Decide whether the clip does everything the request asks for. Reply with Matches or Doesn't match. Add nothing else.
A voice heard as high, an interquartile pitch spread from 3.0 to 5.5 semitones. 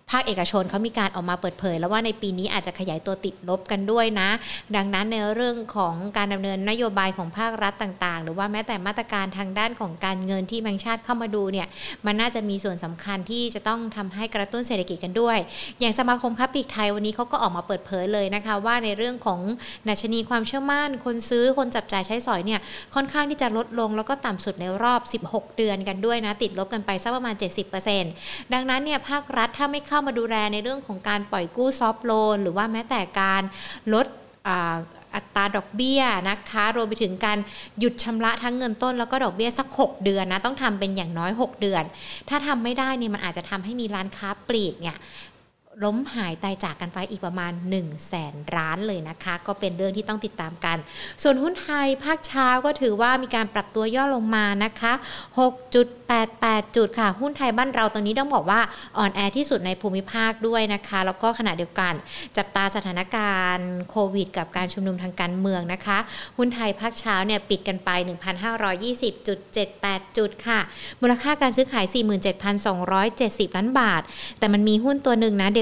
Matches